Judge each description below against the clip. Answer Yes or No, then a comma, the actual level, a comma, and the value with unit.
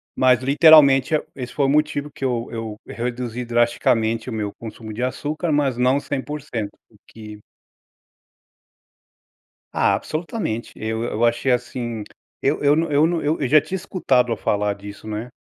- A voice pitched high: No, low, 125 Hz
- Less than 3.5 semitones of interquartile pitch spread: No, average, 4.4 semitones